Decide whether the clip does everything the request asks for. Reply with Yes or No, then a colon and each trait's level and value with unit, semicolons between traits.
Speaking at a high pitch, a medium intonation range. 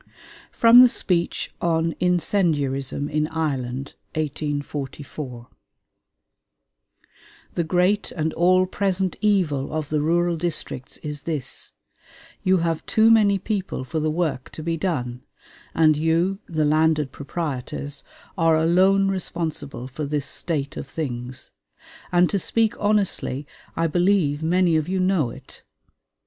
No: medium, 160 Hz; average, 3.9 semitones